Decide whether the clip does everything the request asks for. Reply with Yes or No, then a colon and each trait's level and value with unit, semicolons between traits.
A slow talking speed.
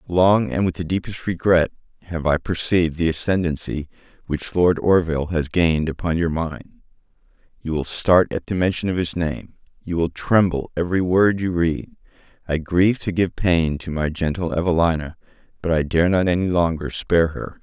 No: average, 165 wpm